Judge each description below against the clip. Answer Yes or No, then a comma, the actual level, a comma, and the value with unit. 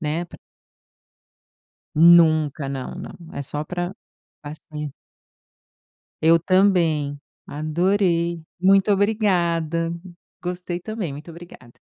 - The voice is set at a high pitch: No, medium, 170 Hz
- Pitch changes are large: No, average, 2.8 semitones